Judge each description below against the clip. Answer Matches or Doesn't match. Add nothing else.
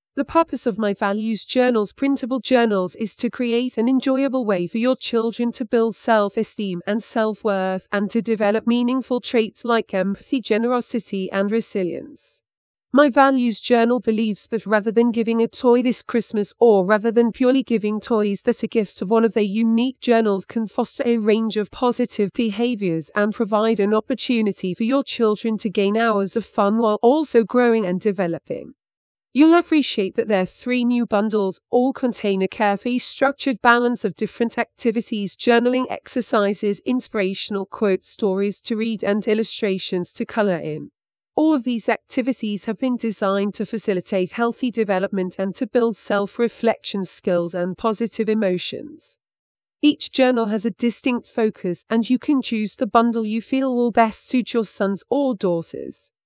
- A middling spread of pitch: Matches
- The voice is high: Matches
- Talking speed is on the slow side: Doesn't match